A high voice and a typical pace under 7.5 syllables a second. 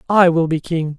No: medium, 165 Hz; 4.9 syllables/s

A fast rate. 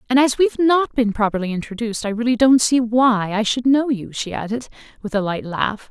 Yes: fast, 225 wpm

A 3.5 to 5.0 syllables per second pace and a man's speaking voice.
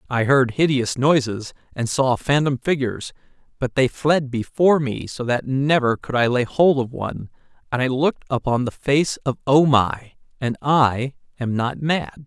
Yes: 4.5 syllables/s; male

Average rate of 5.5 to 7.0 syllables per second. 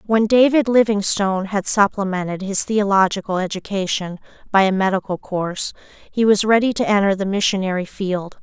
No: 5.3 syllables/s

